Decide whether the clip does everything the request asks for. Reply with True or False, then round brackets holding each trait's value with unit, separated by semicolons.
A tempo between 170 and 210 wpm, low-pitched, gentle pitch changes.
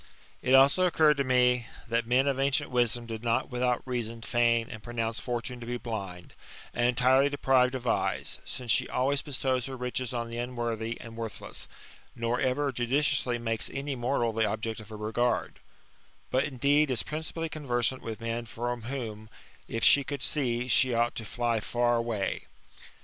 True (175 wpm; 120 Hz; 2.2 semitones)